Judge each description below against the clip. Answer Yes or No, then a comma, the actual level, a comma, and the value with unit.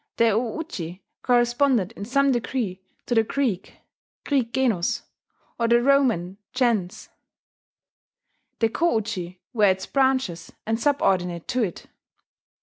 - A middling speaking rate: No, slow, 125 wpm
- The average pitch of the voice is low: No, high, 230 Hz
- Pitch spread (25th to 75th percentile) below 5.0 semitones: No, wide, 5.5 semitones